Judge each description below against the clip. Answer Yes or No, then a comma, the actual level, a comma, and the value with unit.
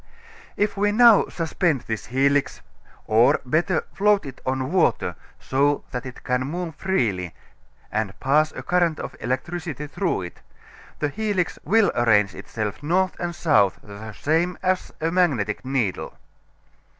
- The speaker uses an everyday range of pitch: No, wide, 6.4 semitones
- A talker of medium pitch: Yes, medium, 145 Hz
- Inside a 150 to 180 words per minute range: No, average, 140 wpm